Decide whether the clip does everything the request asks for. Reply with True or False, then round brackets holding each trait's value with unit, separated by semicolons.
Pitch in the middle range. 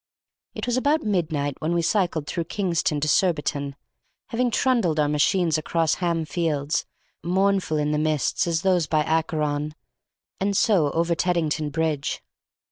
True (165 Hz)